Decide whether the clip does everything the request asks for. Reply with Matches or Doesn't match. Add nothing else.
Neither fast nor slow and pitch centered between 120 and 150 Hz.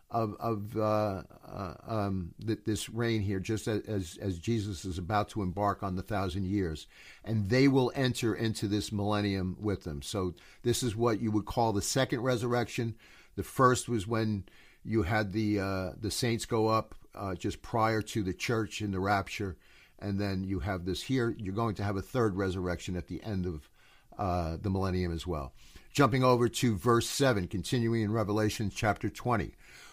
Doesn't match